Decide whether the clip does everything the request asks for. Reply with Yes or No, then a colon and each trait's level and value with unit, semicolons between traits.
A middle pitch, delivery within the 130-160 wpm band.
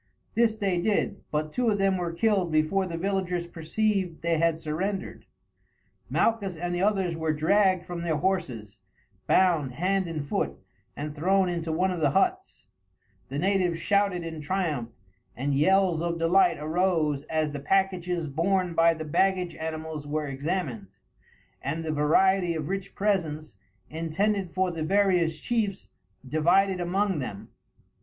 Yes: medium, 170 Hz; average, 150 wpm